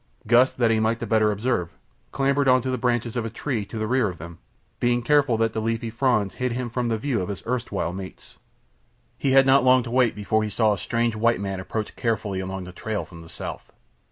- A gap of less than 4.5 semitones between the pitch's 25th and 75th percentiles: Yes, average, 3.2 semitones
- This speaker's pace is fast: Yes, fast, 235 wpm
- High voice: No, low, 115 Hz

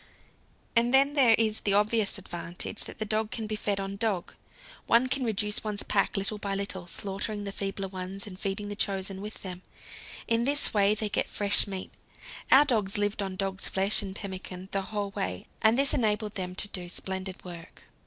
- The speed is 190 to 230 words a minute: Yes, average, 195 wpm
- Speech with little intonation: Yes, narrow, 2.1 semitones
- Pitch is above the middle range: Yes, high, 200 Hz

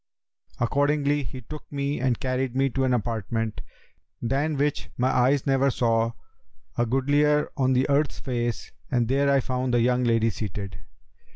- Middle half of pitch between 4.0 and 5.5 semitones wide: No, average, 2.8 semitones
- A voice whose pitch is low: Yes, low, 130 Hz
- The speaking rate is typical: Yes, average, 160 wpm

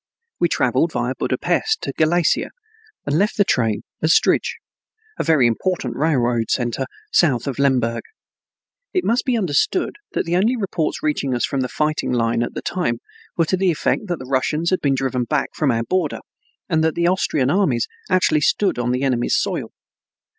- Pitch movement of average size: No, wide, 6.1 semitones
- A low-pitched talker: No, medium, 150 Hz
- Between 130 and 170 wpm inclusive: No, average, 180 wpm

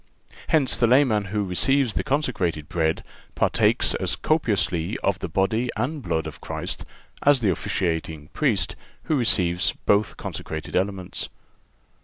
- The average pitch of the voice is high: No, low, 100 Hz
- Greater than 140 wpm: No, slow, 135 wpm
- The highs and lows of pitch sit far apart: Yes, wide, 6.4 semitones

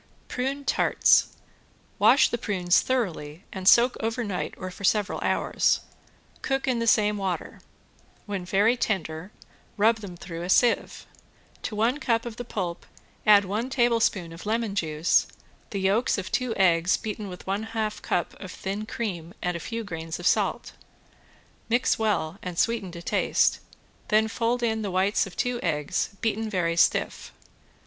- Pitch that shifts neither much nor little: Yes, average, 4.1 semitones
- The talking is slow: No, average, 160 wpm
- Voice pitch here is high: Yes, high, 205 Hz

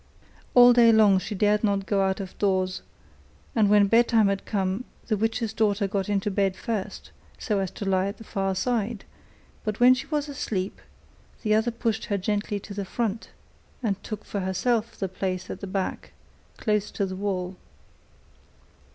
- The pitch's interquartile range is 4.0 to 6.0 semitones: No, narrow, 2.5 semitones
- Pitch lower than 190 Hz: No, high, 205 Hz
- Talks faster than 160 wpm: Yes, average, 175 wpm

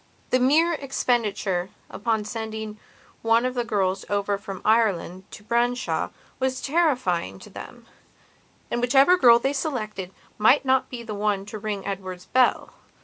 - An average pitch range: Yes, average, 4.1 semitones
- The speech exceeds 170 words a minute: No, average, 145 wpm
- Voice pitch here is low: No, high, 220 Hz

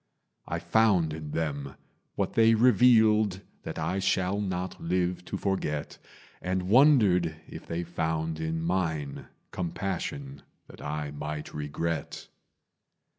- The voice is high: No, very low, 85 Hz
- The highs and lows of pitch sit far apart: No, average, 3.8 semitones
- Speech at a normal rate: No, slow, 120 wpm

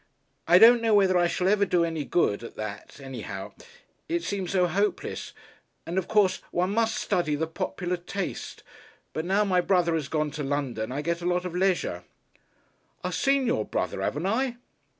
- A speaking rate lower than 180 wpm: No, average, 185 wpm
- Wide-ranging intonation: No, average, 4.5 semitones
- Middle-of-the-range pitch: Yes, medium, 175 Hz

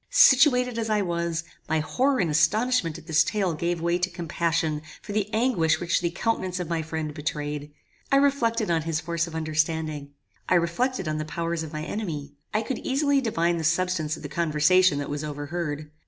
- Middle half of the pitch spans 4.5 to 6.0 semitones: Yes, average, 5.1 semitones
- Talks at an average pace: Yes, average, 195 wpm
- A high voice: No, medium, 170 Hz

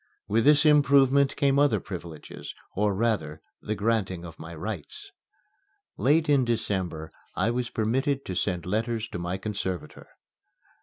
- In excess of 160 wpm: No, average, 140 wpm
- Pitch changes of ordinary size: No, wide, 6.6 semitones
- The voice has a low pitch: Yes, low, 110 Hz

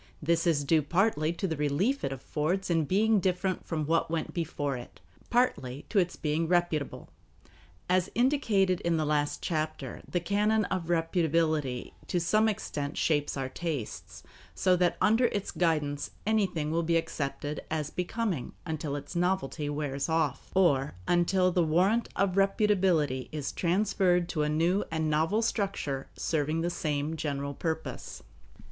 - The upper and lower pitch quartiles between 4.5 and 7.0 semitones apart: No, average, 3.9 semitones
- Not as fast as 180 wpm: Yes, average, 155 wpm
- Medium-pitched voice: Yes, medium, 165 Hz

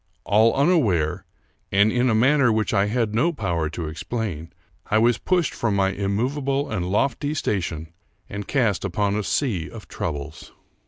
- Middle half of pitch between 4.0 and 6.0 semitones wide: Yes, average, 4.8 semitones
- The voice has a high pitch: No, low, 105 Hz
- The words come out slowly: No, average, 160 wpm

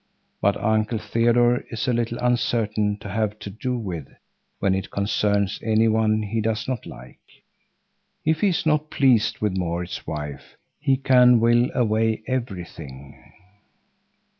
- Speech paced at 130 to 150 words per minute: Yes, average, 140 wpm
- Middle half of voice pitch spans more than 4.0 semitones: No, average, 3.2 semitones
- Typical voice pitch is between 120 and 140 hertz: No, low, 110 Hz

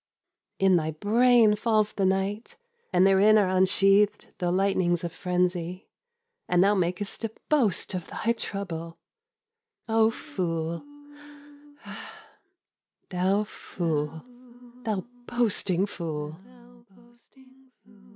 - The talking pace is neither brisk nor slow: No, slow, 95 wpm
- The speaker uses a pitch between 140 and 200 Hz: Yes, high, 190 Hz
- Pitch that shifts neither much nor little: Yes, average, 3.1 semitones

